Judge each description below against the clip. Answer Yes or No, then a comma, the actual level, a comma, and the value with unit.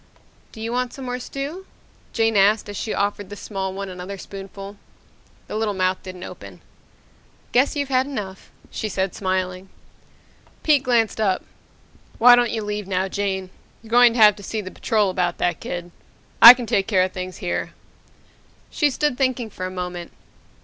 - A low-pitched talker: No, high, 205 Hz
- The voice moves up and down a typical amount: Yes, average, 4.3 semitones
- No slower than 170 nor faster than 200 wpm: Yes, average, 175 wpm